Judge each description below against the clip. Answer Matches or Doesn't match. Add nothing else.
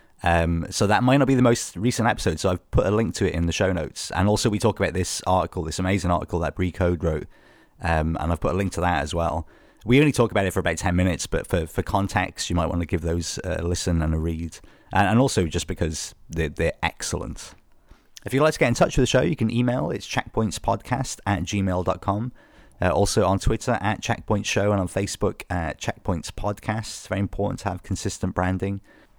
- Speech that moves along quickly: Matches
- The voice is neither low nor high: Doesn't match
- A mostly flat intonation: Doesn't match